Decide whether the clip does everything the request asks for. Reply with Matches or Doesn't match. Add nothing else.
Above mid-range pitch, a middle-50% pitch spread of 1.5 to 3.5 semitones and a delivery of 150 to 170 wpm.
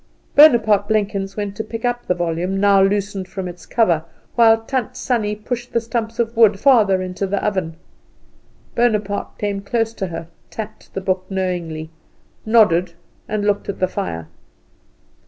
Matches